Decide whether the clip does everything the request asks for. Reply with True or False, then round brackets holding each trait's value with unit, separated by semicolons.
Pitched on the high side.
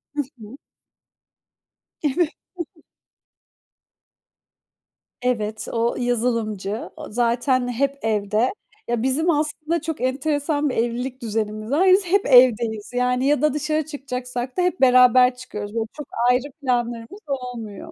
True (250 Hz)